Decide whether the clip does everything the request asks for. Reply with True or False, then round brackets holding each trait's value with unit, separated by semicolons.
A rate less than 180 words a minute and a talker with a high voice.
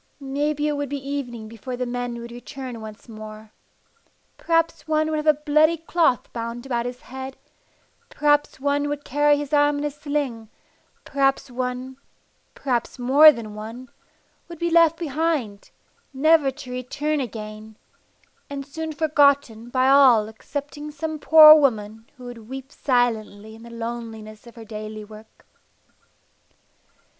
True (145 wpm; 265 Hz)